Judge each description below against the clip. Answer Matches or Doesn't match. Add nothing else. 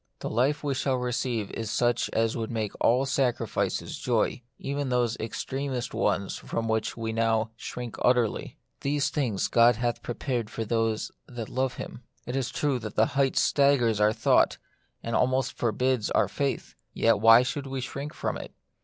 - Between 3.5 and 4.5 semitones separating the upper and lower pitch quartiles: Doesn't match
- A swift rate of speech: Doesn't match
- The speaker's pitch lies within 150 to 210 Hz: Doesn't match